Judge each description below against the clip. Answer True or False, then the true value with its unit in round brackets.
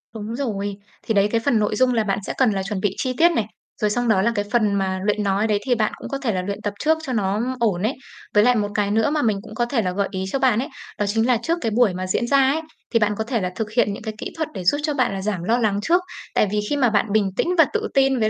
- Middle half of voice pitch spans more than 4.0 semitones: False (3.5 semitones)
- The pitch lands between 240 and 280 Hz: False (220 Hz)